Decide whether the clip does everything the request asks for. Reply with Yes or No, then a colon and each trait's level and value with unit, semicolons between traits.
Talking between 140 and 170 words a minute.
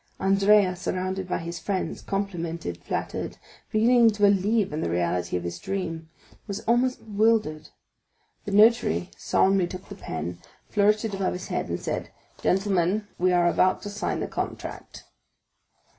Yes: average, 150 wpm